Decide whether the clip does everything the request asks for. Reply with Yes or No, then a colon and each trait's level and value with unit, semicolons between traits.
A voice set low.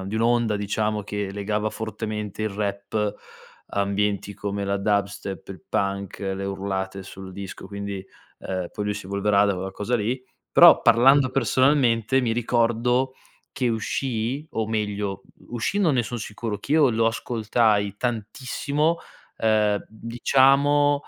Yes: low, 105 Hz